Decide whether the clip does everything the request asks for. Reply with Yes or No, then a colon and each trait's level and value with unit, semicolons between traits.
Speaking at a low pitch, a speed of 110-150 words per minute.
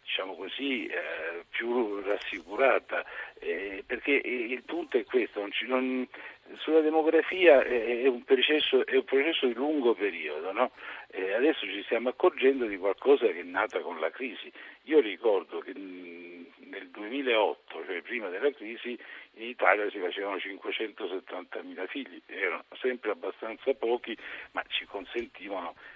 No: very high, 385 Hz; average, 145 wpm